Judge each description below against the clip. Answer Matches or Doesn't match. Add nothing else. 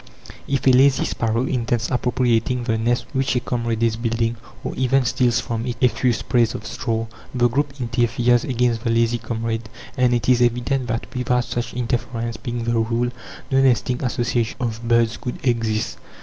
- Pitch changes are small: Matches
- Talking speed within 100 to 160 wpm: Doesn't match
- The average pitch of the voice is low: Matches